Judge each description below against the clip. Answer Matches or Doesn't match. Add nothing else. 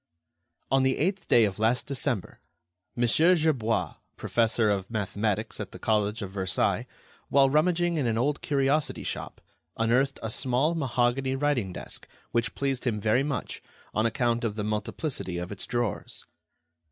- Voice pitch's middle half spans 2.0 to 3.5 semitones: Doesn't match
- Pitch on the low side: Matches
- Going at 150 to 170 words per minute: Matches